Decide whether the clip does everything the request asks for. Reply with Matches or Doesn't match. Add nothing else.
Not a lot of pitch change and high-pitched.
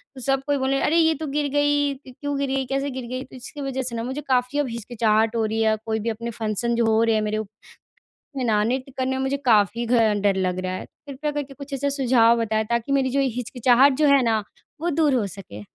Doesn't match